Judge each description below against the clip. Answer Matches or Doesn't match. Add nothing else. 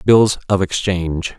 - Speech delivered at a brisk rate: Doesn't match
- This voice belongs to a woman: Doesn't match